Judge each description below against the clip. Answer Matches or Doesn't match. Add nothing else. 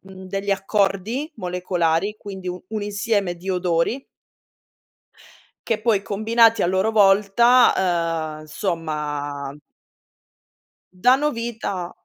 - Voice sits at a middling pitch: Doesn't match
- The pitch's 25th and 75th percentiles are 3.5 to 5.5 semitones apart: Matches